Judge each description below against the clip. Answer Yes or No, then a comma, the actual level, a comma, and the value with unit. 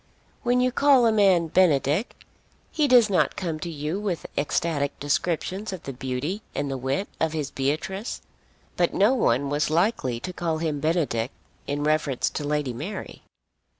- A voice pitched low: No, medium, 160 Hz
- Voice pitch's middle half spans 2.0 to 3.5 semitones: No, average, 5.3 semitones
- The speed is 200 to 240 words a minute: No, average, 165 wpm